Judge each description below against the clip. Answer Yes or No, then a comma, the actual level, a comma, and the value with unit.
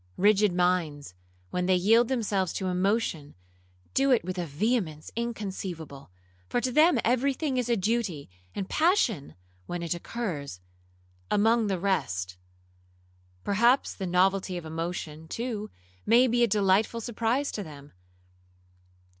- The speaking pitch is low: No, high, 195 Hz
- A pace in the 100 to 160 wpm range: Yes, slow, 135 wpm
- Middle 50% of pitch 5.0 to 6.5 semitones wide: Yes, wide, 5.4 semitones